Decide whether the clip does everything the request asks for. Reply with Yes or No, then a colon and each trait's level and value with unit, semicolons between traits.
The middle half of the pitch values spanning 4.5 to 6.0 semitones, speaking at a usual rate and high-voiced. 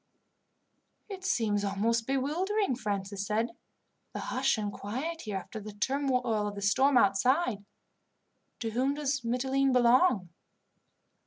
No: average, 4.8 semitones; slow, 125 wpm; high, 240 Hz